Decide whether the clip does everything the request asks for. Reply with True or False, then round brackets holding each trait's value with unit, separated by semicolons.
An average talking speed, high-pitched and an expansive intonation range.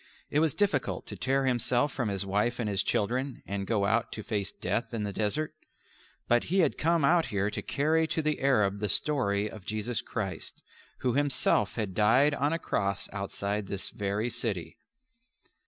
False (185 wpm; 115 Hz; 5.7 semitones)